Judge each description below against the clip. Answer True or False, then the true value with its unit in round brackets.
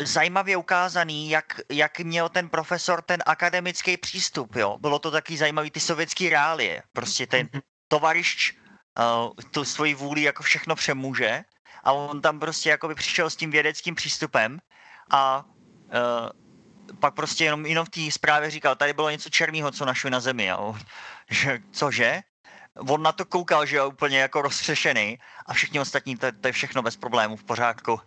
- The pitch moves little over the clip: False (3.4 semitones)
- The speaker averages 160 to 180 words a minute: True (170 wpm)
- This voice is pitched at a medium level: True (150 Hz)